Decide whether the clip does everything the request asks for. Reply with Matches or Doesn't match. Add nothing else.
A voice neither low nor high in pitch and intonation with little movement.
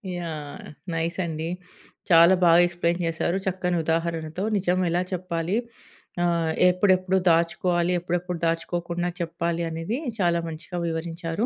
Matches